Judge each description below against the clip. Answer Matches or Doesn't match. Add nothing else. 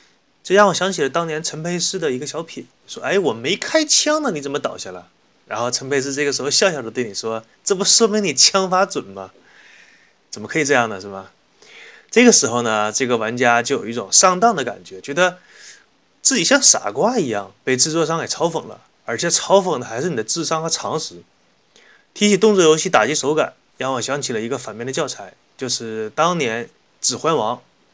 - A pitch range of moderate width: Doesn't match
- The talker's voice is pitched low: Doesn't match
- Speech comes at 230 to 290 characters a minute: Doesn't match